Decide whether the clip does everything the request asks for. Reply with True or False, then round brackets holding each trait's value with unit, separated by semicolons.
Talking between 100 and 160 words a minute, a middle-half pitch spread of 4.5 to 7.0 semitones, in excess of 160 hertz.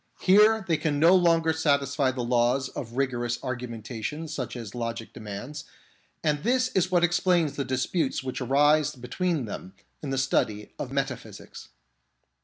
False (155 wpm; 5.1 semitones; 140 Hz)